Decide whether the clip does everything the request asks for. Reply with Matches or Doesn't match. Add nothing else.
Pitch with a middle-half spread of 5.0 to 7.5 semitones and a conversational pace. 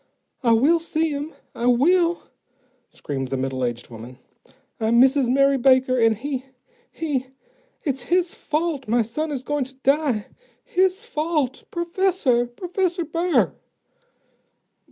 Doesn't match